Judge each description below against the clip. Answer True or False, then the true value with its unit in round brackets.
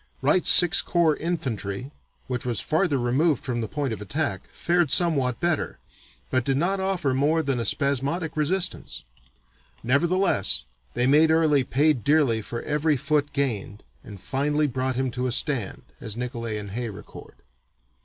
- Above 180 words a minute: False (155 wpm)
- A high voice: False (140 Hz)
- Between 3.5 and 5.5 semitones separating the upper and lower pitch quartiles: True (4.6 semitones)